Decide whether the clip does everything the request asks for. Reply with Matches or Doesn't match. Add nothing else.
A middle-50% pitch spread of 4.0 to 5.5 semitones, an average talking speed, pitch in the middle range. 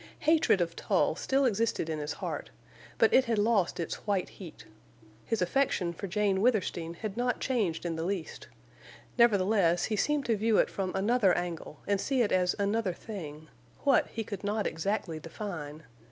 Doesn't match